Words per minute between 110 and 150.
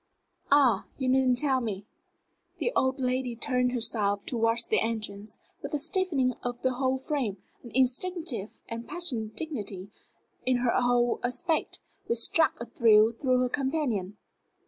Yes: average, 145 wpm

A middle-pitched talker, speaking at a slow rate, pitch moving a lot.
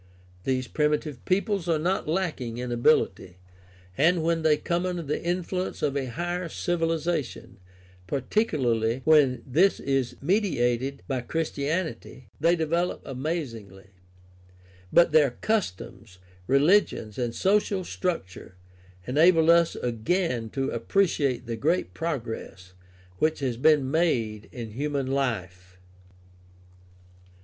Yes: medium, 145 Hz; slow, 115 wpm; wide, 5.8 semitones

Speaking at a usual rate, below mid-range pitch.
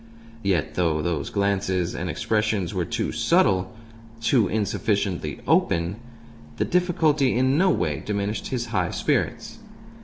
No: slow, 125 wpm; low, 100 Hz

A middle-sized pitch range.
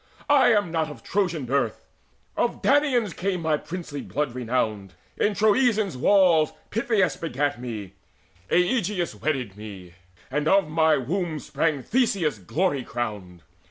No: wide, 7.7 semitones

